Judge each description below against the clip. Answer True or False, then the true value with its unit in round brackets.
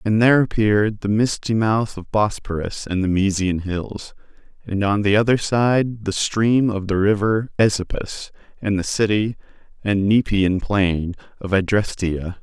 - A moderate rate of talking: True (150 wpm)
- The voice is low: True (105 Hz)